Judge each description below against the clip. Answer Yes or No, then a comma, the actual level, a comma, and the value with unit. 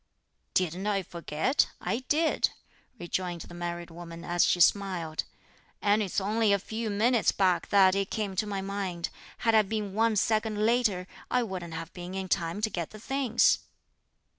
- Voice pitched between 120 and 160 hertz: No, high, 195 Hz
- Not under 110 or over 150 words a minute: No, average, 170 wpm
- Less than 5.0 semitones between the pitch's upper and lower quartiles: Yes, average, 3.7 semitones